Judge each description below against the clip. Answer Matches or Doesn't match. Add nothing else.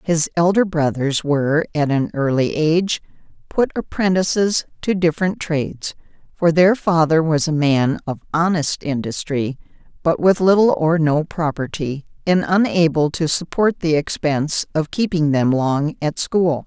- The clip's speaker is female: Matches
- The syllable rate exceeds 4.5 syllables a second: Doesn't match